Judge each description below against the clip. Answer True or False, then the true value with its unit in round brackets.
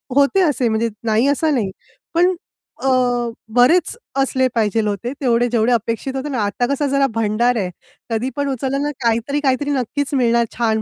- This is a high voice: True (250 Hz)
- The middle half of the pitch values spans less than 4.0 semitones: True (3.6 semitones)